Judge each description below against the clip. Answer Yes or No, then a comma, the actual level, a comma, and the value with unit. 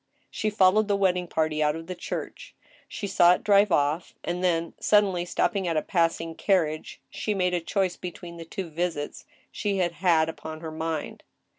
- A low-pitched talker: No, medium, 175 Hz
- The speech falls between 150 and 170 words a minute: No, average, 180 wpm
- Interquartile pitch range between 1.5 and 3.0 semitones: Yes, average, 2.7 semitones